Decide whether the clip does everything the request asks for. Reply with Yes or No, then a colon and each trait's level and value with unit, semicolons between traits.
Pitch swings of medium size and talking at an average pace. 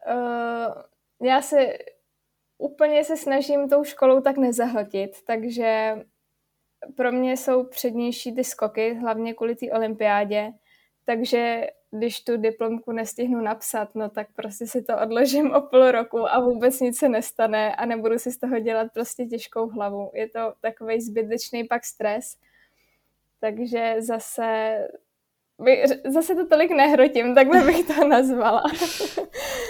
Yes: average, 3.0 semitones; average, 135 wpm